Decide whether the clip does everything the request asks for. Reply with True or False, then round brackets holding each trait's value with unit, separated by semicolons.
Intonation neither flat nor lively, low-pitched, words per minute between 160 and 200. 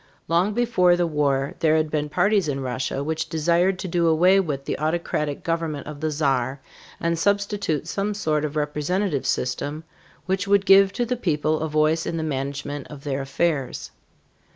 False (3.7 semitones; 155 Hz; 175 wpm)